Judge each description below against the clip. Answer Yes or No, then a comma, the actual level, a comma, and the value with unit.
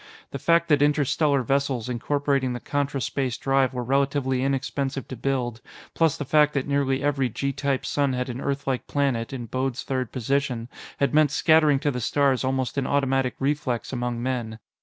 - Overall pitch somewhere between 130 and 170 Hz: Yes, low, 135 Hz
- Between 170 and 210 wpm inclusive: Yes, average, 180 wpm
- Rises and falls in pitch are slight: Yes, narrow, 1.9 semitones